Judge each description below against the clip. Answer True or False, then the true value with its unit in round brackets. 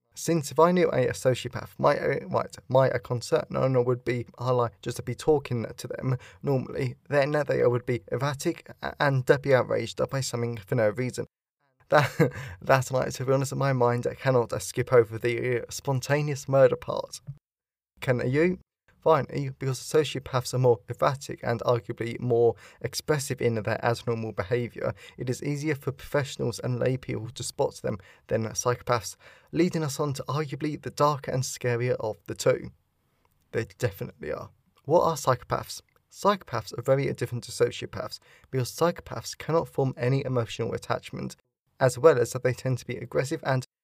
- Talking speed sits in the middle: True (180 wpm)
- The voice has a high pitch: False (125 Hz)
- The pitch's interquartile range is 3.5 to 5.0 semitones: False (2.7 semitones)